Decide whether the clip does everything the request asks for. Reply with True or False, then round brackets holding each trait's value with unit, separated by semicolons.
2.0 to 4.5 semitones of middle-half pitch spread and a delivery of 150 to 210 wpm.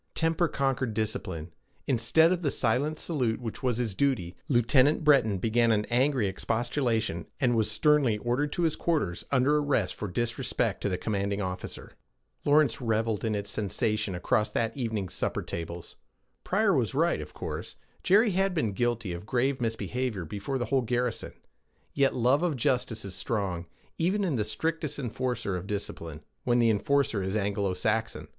False (5.2 semitones; 165 wpm)